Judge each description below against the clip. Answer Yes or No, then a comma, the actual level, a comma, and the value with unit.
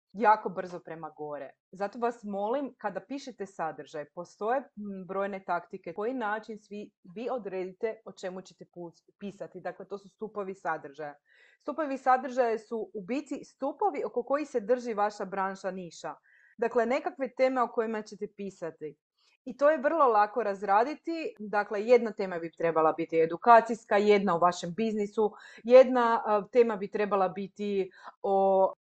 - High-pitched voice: Yes, high, 205 Hz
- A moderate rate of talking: Yes, average, 145 wpm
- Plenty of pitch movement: No, average, 4.3 semitones